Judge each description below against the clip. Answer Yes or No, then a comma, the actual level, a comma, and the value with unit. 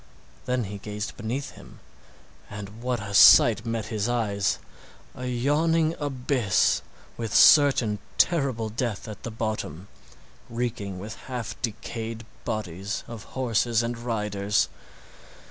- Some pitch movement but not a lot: Yes, average, 3.0 semitones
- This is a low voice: Yes, low, 115 Hz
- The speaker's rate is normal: No, slow, 125 wpm